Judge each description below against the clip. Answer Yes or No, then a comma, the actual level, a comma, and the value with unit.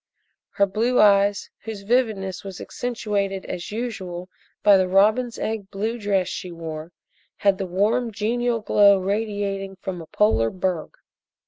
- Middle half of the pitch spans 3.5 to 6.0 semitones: No, narrow, 2.5 semitones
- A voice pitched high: Yes, high, 200 Hz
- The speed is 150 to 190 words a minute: No, average, 140 wpm